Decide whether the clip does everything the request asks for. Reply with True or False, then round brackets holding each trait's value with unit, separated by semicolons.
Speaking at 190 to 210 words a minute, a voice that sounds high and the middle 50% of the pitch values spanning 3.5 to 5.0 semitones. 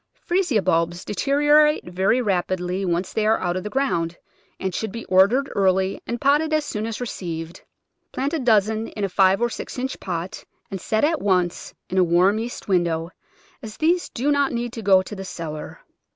False (195 wpm; 205 Hz; 5.6 semitones)